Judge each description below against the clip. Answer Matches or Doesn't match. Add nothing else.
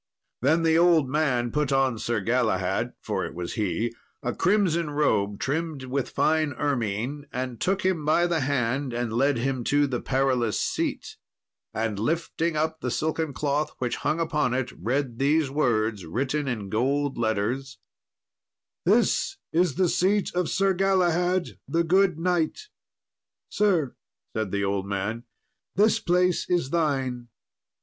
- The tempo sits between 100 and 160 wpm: Matches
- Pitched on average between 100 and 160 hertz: Matches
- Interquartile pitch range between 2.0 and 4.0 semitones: Doesn't match